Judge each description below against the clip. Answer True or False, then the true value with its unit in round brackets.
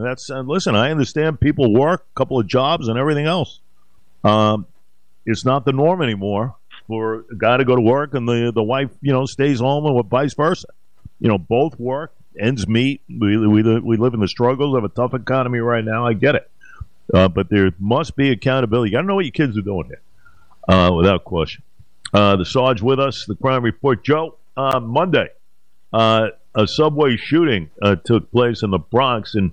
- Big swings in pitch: False (4.0 semitones)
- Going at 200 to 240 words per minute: True (205 wpm)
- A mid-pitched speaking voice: False (120 Hz)